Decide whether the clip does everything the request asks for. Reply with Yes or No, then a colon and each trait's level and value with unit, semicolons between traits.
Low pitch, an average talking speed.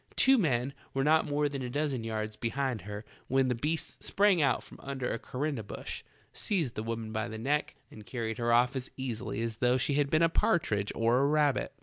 No: low, 125 Hz; fast, 220 wpm